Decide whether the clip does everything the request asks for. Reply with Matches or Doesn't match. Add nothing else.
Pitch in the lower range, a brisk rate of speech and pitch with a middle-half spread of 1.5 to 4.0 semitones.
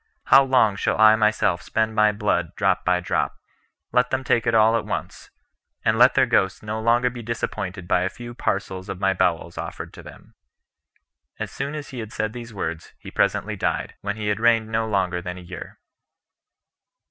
Doesn't match